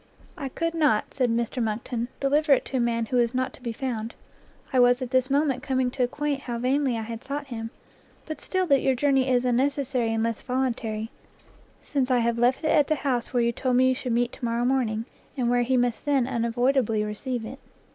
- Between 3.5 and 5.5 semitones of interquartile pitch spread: No, narrow, 2.4 semitones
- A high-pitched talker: Yes, very high, 250 Hz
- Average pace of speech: No, fast, 220 wpm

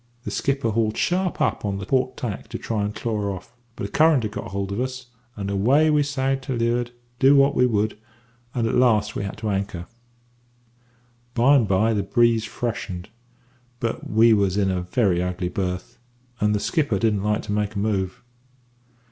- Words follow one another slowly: No, average, 195 wpm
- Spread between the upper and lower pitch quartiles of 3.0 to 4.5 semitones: Yes, average, 3.9 semitones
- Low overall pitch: Yes, low, 110 Hz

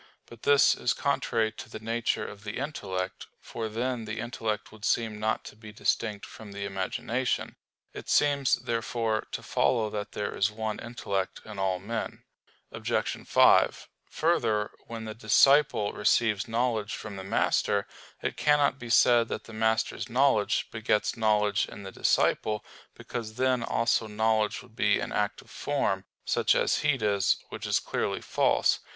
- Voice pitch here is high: No, low, 110 Hz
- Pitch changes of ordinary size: No, narrow, 2.1 semitones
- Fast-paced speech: No, average, 160 wpm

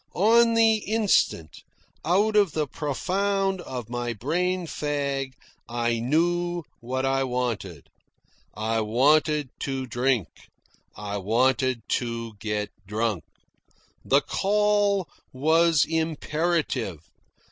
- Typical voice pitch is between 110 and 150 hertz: Yes, medium, 140 Hz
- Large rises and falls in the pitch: Yes, wide, 6.9 semitones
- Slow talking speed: Yes, slow, 100 wpm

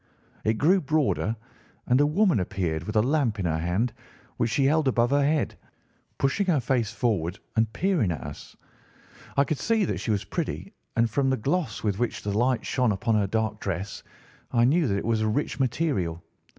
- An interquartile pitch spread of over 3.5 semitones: Yes, wide, 5.5 semitones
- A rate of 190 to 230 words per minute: Yes, average, 200 wpm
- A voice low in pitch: Yes, low, 120 Hz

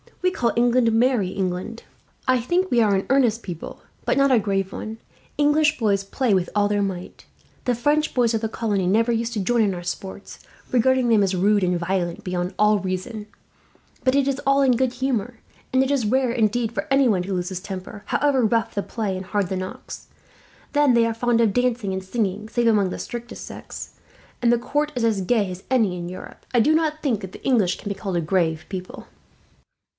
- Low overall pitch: No, high, 225 Hz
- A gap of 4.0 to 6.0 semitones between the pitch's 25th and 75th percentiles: Yes, average, 4.5 semitones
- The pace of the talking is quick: Yes, fast, 215 wpm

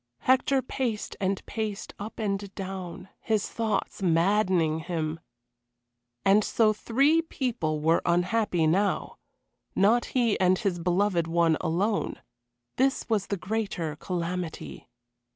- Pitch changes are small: No, average, 4.2 semitones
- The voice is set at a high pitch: Yes, high, 195 Hz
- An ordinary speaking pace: No, slow, 115 wpm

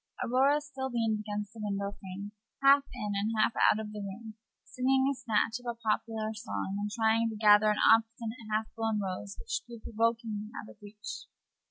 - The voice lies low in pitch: No, high, 220 Hz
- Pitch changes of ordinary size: No, narrow, 1.8 semitones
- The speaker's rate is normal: Yes, average, 190 wpm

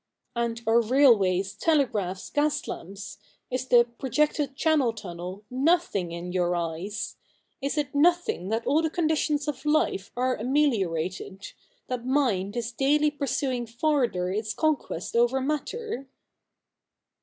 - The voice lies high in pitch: Yes, high, 245 Hz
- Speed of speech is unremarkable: No, slow, 130 wpm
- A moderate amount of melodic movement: No, wide, 6.7 semitones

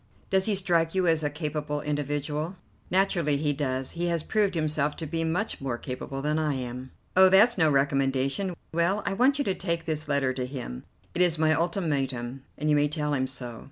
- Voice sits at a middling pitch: Yes, medium, 150 Hz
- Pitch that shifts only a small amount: No, average, 4.0 semitones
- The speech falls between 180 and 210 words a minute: Yes, fast, 205 wpm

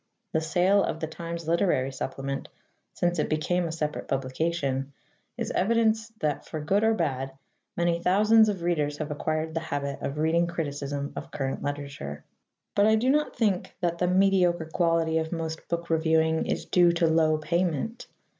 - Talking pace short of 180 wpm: Yes, average, 170 wpm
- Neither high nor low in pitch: Yes, medium, 165 Hz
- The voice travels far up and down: No, average, 3.1 semitones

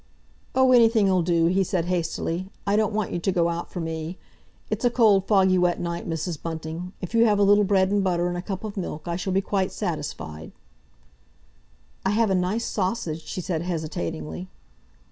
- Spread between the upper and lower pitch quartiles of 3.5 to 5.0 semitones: No, average, 3.1 semitones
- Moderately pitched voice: Yes, medium, 180 Hz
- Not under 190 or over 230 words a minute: Yes, average, 195 wpm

